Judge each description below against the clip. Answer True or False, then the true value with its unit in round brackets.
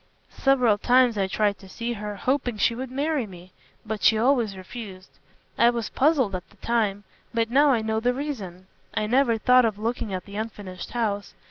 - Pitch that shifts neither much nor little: True (3.5 semitones)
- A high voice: True (225 Hz)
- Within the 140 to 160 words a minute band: False (195 wpm)